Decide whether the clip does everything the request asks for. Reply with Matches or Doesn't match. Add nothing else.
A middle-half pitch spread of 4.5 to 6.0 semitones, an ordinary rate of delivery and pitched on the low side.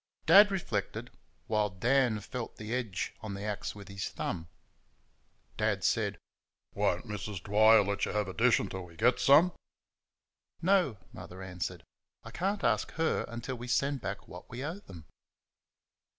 Matches